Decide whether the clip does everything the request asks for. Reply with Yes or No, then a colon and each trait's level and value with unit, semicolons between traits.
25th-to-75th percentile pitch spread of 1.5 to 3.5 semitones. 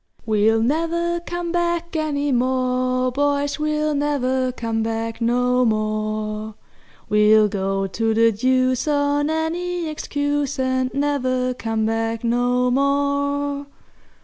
No: average, 4.2 semitones